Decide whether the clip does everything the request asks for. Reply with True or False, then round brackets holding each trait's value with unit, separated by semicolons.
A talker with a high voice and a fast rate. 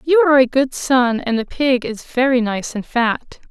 True (260 Hz; 225 wpm)